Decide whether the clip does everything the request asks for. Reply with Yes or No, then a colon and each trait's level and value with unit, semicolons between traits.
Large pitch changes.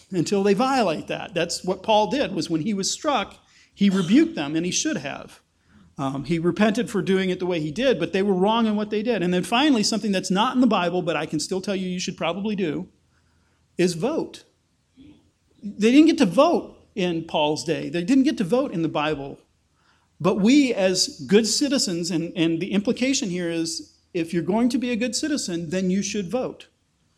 Yes: wide, 5.8 semitones